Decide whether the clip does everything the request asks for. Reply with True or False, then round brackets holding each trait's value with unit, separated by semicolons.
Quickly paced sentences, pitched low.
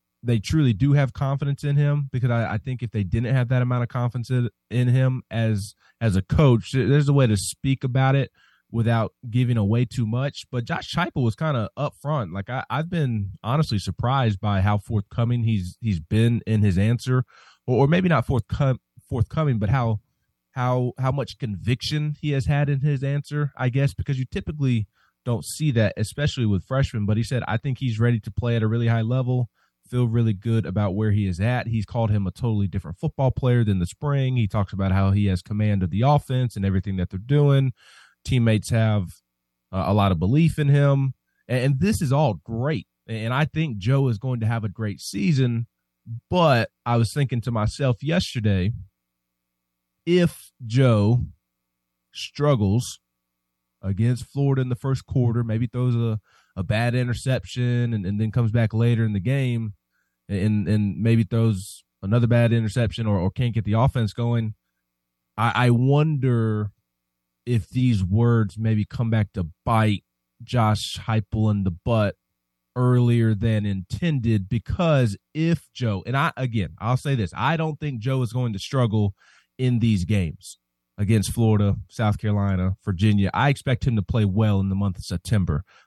False (185 wpm; 115 Hz)